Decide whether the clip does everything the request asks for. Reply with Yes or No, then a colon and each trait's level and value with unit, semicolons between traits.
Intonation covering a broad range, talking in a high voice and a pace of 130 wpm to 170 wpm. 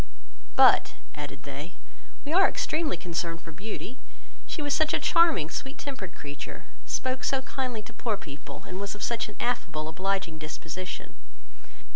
Yes: wide, 8.5 semitones; high, 195 Hz; average, 155 wpm